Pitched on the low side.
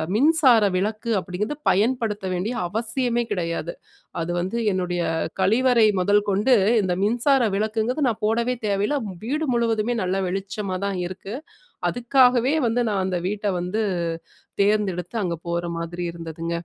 No: high, 210 Hz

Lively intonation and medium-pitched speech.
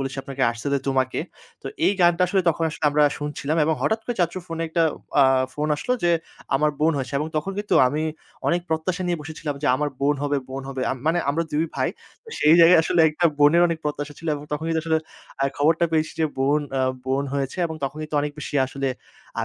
No: average, 2.7 semitones; medium, 150 Hz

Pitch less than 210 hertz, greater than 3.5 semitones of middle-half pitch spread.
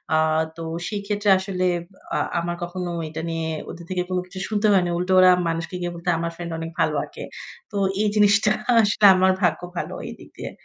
No: medium, 185 Hz; average, 3.0 semitones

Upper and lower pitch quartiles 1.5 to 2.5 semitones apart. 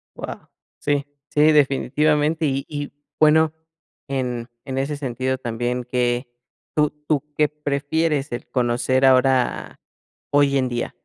No: average, 2.9 semitones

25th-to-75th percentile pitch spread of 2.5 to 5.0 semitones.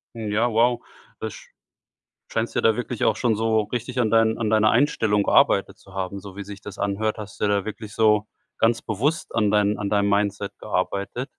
No: narrow, 1.8 semitones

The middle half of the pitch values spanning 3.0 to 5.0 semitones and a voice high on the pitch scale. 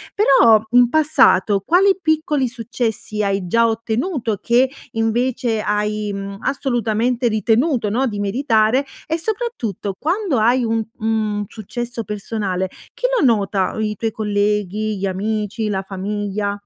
Yes: average, 3.3 semitones; high, 220 Hz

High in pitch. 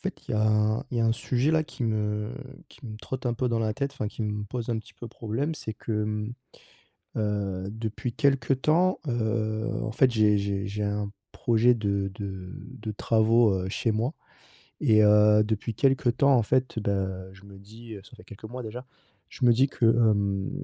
No: low, 110 Hz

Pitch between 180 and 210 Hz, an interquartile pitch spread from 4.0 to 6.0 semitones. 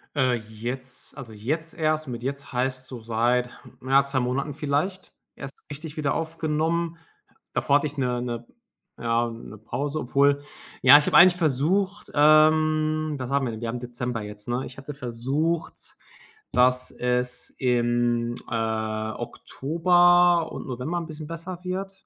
No: low, 135 Hz; average, 4.3 semitones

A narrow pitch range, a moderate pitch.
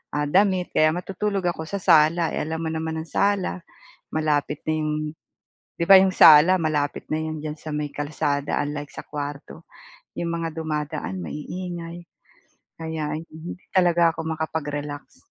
Yes: narrow, 2.3 semitones; medium, 160 Hz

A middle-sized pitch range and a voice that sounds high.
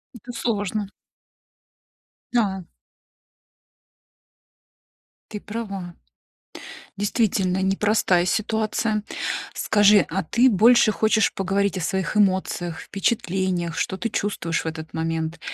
Yes: average, 3.0 semitones; high, 195 Hz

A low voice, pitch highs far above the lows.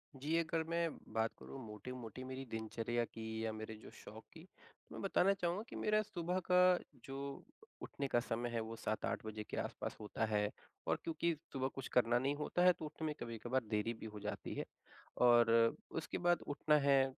Yes: low, 130 Hz; wide, 6.2 semitones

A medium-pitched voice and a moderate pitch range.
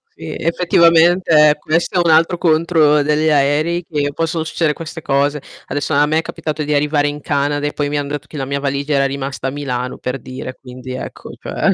No: medium, 145 Hz; narrow, 2.2 semitones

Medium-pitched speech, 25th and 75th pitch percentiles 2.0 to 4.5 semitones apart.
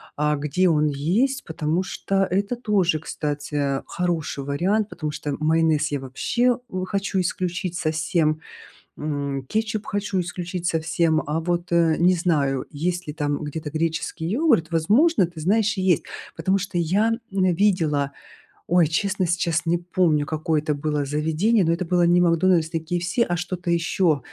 Yes: medium, 170 Hz; average, 3.3 semitones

